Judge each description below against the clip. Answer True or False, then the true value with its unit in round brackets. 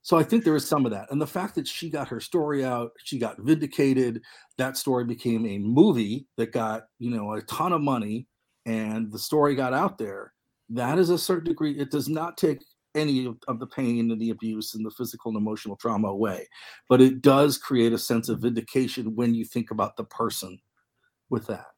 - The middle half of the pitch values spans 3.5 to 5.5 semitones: True (4.0 semitones)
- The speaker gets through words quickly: True (220 wpm)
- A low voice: True (125 Hz)